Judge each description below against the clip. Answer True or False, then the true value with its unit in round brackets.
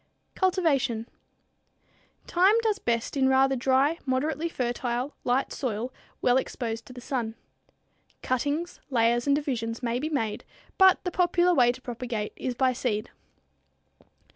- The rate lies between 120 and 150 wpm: True (140 wpm)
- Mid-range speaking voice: False (260 Hz)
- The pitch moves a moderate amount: True (3.7 semitones)